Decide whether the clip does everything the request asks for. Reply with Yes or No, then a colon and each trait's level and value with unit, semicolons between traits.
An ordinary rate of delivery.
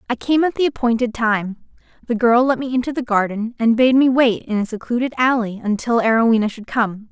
No: fast, 210 wpm